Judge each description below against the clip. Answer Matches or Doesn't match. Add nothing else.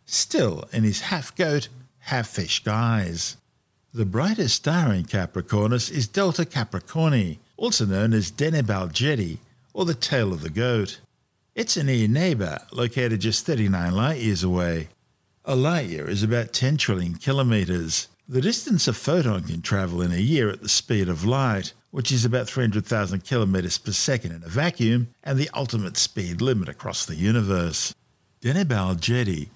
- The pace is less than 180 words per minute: Matches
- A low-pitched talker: Matches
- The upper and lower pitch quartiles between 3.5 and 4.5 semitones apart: Doesn't match